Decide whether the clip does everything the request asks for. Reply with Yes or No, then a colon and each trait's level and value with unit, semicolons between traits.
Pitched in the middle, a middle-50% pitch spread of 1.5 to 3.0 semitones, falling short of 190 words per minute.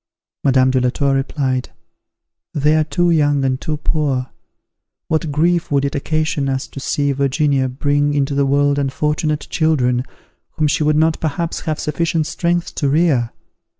Yes: medium, 145 Hz; narrow, 2.4 semitones; average, 160 wpm